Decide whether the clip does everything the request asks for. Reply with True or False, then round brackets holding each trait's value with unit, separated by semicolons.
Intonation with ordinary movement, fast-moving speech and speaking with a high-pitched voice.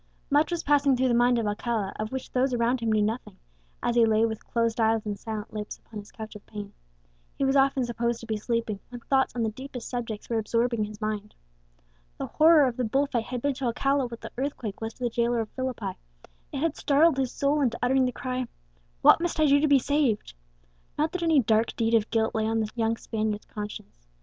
True (3.4 semitones; 235 wpm; 235 Hz)